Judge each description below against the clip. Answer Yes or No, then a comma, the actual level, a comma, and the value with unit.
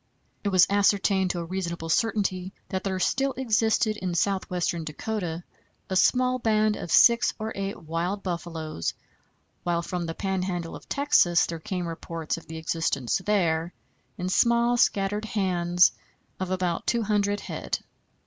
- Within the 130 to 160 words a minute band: Yes, average, 150 wpm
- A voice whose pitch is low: No, medium, 185 Hz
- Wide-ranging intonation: No, average, 3.6 semitones